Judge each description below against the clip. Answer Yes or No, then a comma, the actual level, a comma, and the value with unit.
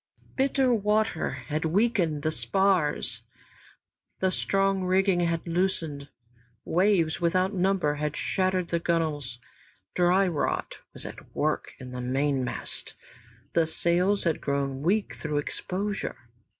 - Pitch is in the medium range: Yes, medium, 170 Hz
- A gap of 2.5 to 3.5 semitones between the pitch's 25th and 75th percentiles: No, average, 4.4 semitones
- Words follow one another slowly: Yes, slow, 120 wpm